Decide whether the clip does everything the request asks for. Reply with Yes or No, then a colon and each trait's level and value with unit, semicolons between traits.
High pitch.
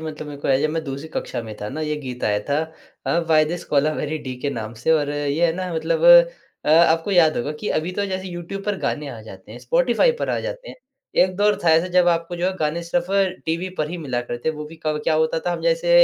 No: medium, 160 Hz